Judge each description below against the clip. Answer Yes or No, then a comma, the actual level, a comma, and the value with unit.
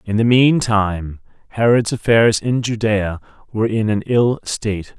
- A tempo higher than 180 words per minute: No, average, 155 wpm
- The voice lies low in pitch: Yes, low, 110 Hz